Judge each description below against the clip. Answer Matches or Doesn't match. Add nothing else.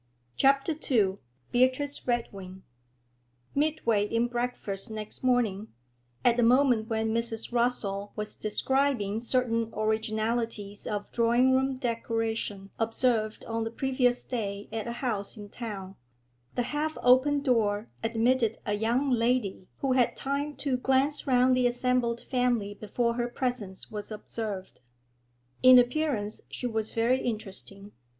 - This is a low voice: Doesn't match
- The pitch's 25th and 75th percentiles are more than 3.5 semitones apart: Doesn't match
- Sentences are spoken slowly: Matches